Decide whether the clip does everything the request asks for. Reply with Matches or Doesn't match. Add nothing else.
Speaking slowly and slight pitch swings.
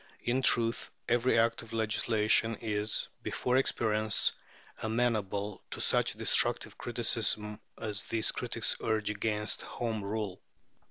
Matches